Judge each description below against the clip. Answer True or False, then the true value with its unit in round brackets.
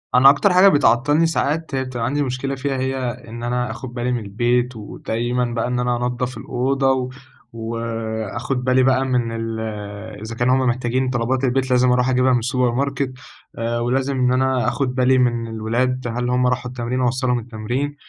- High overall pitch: False (125 Hz)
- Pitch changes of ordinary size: False (1.7 semitones)